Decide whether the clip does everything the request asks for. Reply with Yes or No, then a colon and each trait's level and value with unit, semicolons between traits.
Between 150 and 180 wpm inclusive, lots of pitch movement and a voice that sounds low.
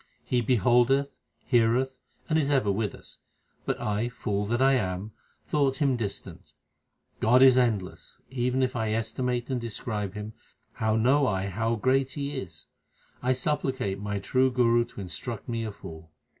No: average, 160 wpm; average, 3.8 semitones; low, 120 Hz